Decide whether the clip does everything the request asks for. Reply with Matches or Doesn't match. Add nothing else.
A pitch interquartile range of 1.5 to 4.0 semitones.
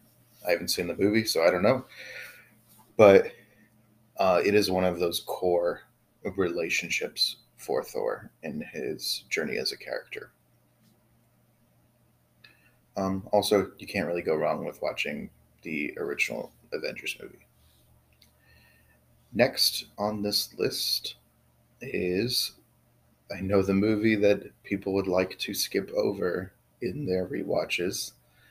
Matches